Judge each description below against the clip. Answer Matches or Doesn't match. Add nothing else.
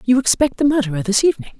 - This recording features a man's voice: Doesn't match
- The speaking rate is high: Matches